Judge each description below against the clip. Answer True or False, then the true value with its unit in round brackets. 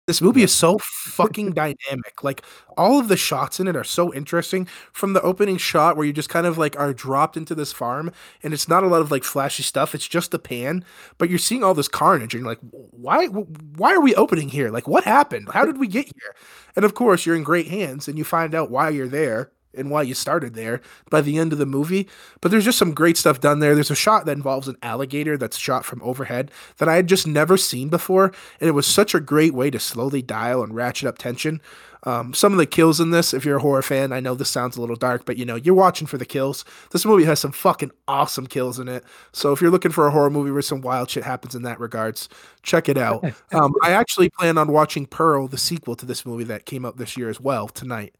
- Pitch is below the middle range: False (150 Hz)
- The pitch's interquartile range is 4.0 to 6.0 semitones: True (4.7 semitones)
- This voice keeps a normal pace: False (260 wpm)